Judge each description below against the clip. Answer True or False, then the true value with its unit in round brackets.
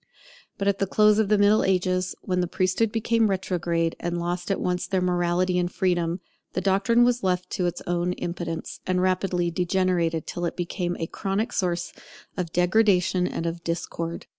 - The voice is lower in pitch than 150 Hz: False (180 Hz)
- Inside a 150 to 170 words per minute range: False (185 wpm)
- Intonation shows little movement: True (1.8 semitones)